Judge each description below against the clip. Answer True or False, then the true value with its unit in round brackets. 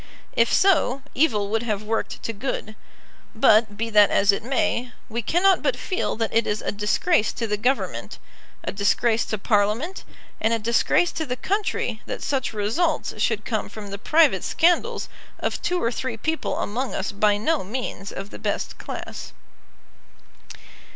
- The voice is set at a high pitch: True (225 Hz)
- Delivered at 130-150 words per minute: False (170 wpm)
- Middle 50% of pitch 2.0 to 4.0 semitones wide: False (4.4 semitones)